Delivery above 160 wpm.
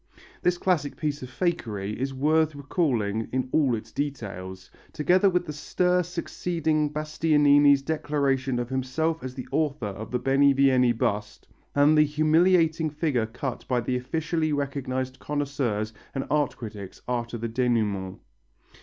No: average, 140 wpm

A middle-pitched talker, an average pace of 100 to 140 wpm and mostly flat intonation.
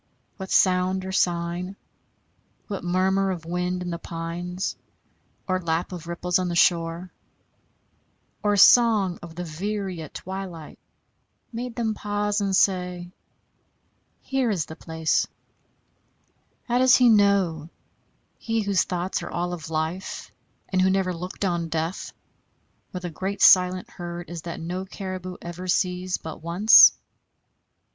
Yes: medium, 180 Hz; slow, 135 wpm; narrow, 2.1 semitones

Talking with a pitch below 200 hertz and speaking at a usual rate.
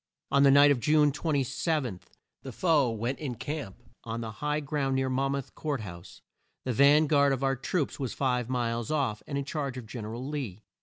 No: low, 135 Hz; fast, 210 wpm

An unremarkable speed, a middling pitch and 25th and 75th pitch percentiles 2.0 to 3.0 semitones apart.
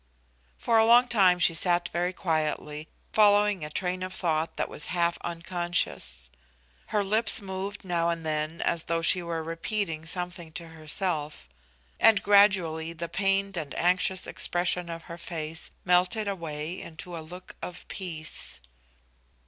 Yes: average, 150 wpm; medium, 175 Hz; average, 2.7 semitones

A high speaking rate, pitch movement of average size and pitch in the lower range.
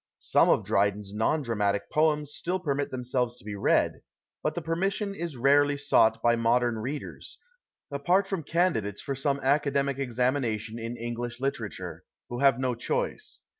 No: average, 155 wpm; average, 4.2 semitones; low, 130 Hz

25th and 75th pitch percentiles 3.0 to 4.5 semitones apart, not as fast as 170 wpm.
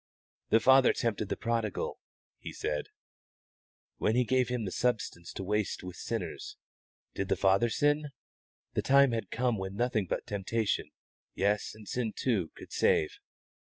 Yes: average, 4.2 semitones; average, 155 wpm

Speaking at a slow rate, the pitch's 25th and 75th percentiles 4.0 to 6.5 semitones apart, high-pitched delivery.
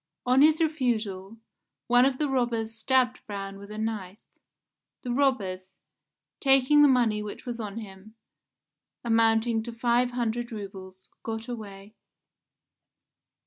No: slow, 120 wpm; average, 3.3 semitones; high, 225 Hz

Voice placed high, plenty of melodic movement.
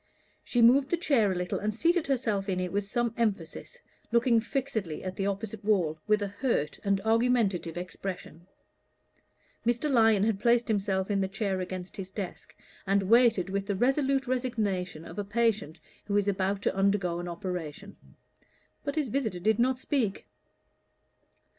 No: high, 205 Hz; average, 3.8 semitones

